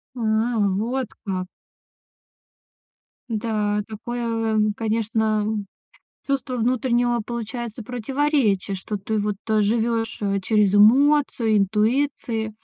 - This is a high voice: Yes, high, 220 Hz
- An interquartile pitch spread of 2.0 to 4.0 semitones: Yes, narrow, 2.5 semitones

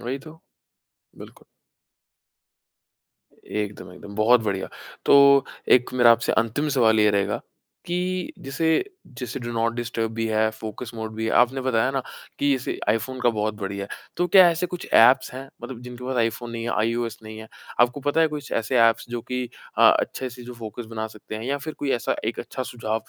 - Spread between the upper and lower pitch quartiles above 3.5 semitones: No, average, 3.0 semitones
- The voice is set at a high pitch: No, low, 120 Hz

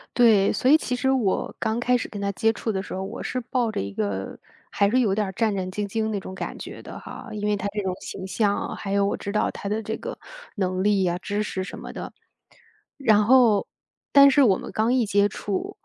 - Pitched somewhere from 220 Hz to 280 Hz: No, high, 210 Hz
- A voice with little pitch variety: No, average, 3.1 semitones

